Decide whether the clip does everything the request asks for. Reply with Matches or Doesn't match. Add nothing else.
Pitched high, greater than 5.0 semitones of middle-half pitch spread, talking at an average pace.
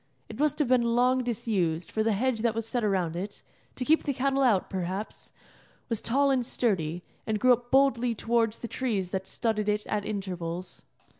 Doesn't match